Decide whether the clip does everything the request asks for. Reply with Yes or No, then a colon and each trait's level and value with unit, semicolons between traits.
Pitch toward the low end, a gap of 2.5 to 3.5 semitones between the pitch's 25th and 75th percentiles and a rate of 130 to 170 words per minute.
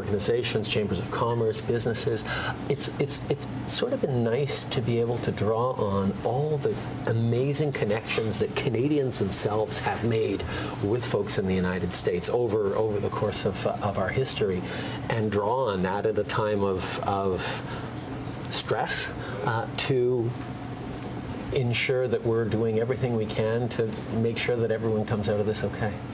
Yes: low, 115 Hz; average, 2.8 semitones; average, 165 wpm